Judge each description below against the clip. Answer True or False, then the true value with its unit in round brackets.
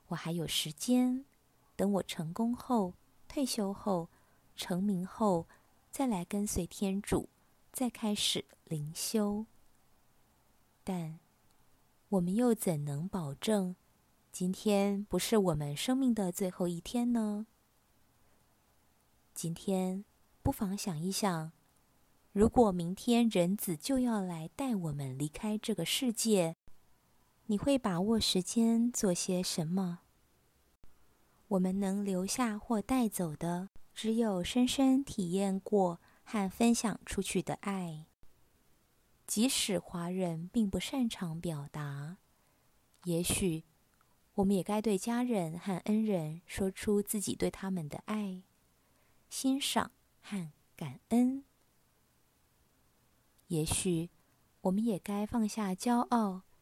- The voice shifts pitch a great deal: False (4.4 semitones)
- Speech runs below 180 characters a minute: True (160 characters per minute)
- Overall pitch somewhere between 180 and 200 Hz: True (190 Hz)